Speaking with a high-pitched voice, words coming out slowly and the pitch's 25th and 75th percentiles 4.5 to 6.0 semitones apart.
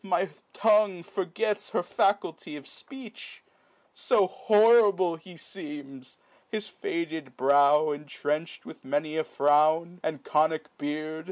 No: medium, 165 Hz; slow, 120 wpm; wide, 5.4 semitones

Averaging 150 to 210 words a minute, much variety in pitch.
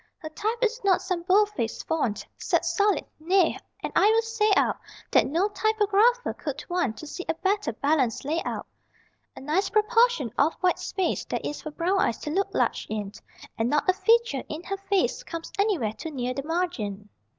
Yes: average, 190 wpm; wide, 6.0 semitones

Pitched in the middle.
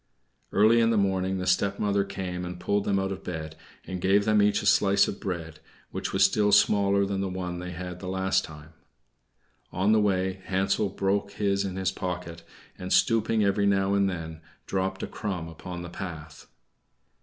No: very low, 95 Hz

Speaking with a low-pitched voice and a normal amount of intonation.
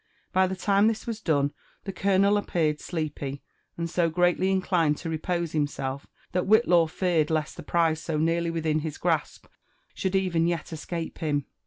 No: medium, 170 Hz; average, 3.1 semitones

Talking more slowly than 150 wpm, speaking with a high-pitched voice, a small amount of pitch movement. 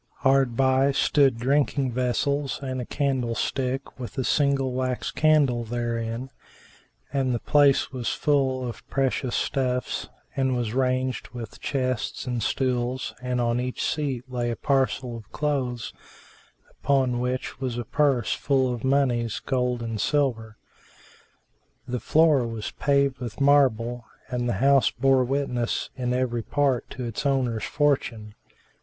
No: average, 140 wpm; low, 130 Hz; narrow, 2.1 semitones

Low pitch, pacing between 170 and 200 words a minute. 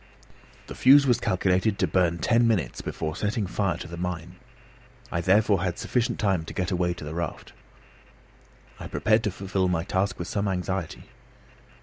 Yes: very low, 95 Hz; average, 175 wpm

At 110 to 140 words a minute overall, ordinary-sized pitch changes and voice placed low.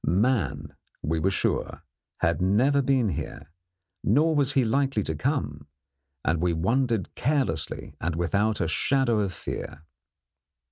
No: slow, 135 wpm; wide, 8.4 semitones; low, 105 Hz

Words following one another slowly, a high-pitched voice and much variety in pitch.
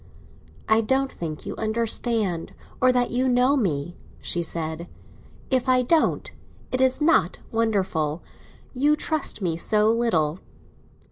Yes: slow, 125 wpm; high, 225 Hz; wide, 6.8 semitones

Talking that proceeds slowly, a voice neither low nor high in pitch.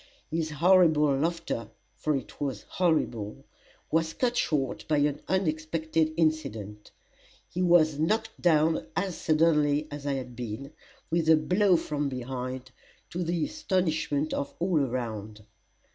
Yes: slow, 130 wpm; medium, 155 Hz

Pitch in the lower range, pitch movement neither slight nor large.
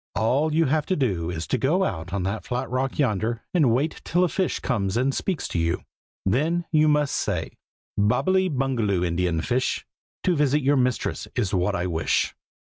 No: low, 125 Hz; wide, 7.6 semitones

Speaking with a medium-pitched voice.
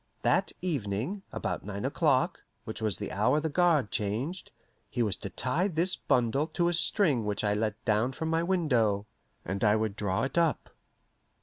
No: low, 125 Hz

